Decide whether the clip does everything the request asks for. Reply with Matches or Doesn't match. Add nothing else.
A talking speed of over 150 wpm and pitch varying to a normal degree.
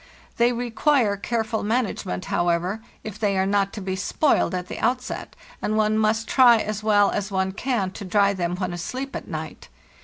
Matches